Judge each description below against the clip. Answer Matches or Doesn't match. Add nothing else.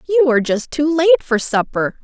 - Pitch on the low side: Doesn't match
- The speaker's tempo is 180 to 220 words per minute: Matches